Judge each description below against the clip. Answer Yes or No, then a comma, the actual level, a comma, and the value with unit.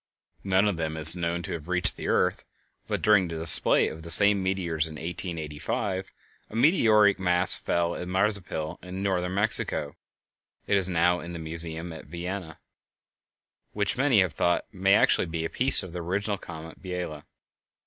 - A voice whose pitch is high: No, very low, 90 Hz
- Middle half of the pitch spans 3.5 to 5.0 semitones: No, average, 2.9 semitones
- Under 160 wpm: No, average, 175 wpm